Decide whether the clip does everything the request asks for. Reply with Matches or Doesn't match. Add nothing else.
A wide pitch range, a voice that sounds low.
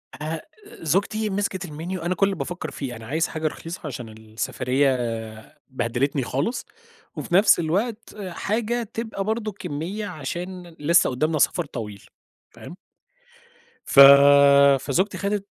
Doesn't match